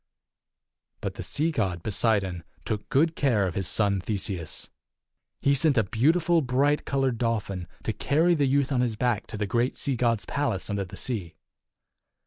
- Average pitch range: No, wide, 5.9 semitones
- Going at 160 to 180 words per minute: Yes, average, 170 wpm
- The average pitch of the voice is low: Yes, low, 115 Hz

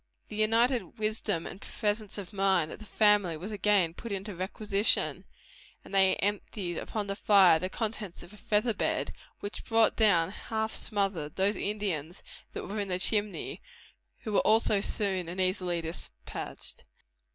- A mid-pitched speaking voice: No, high, 200 Hz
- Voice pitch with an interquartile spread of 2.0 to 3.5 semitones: Yes, narrow, 2.6 semitones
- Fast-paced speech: No, average, 160 wpm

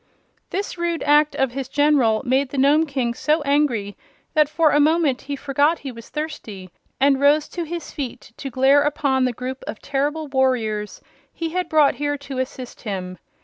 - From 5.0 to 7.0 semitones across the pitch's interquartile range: No, average, 2.8 semitones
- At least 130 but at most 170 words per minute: No, average, 185 wpm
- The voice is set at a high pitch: Yes, very high, 280 Hz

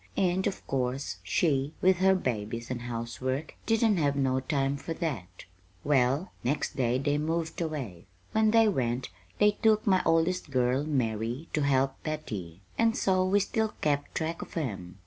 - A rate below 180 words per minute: Yes, average, 160 wpm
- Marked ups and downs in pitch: Yes, wide, 6.0 semitones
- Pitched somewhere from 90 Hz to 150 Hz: Yes, medium, 140 Hz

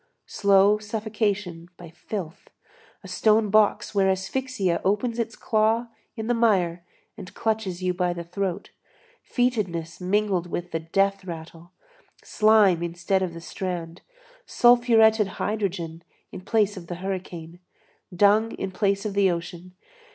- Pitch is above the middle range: Yes, high, 195 Hz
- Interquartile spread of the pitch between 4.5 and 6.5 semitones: No, average, 3.5 semitones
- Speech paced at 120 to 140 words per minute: Yes, slow, 135 wpm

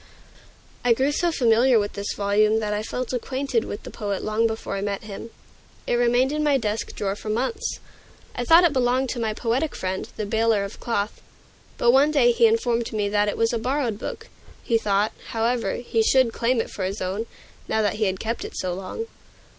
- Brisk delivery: Yes, fast, 210 wpm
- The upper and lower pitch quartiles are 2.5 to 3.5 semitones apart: Yes, average, 3.2 semitones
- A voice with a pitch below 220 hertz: No, high, 230 Hz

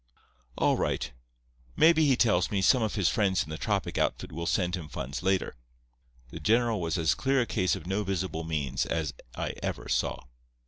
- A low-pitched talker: Yes, very low, 95 Hz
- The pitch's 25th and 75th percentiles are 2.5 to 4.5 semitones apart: No, average, 4.9 semitones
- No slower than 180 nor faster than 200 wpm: Yes, average, 190 wpm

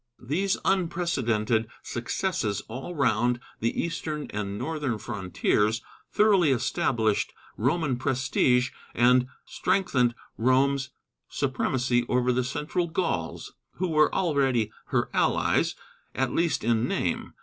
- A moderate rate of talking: No, slow, 105 wpm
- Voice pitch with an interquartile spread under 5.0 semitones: Yes, average, 4.6 semitones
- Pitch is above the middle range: No, low, 130 Hz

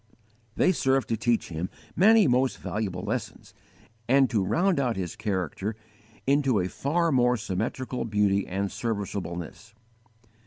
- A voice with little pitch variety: No, average, 5.3 semitones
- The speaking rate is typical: No, slow, 130 wpm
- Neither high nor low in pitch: No, low, 115 Hz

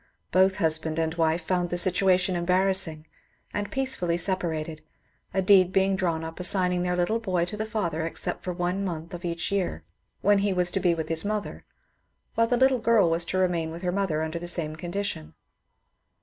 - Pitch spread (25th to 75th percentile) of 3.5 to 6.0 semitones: No, average, 2.7 semitones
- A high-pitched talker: No, medium, 180 Hz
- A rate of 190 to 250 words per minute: Yes, average, 195 wpm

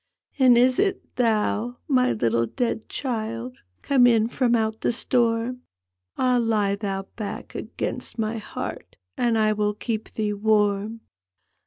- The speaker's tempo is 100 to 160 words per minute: Yes, average, 145 wpm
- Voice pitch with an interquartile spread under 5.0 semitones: Yes, average, 2.8 semitones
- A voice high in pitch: Yes, high, 225 Hz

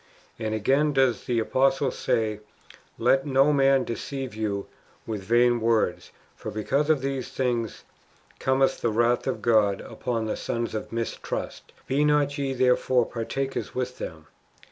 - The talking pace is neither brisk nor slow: Yes, average, 150 wpm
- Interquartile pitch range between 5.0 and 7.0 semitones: No, average, 3.2 semitones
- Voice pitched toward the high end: No, low, 125 Hz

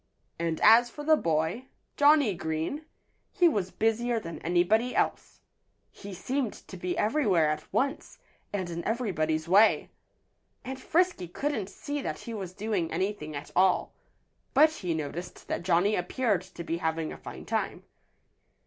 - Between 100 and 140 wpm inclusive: No, average, 150 wpm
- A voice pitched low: No, high, 195 Hz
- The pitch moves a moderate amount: No, wide, 6.6 semitones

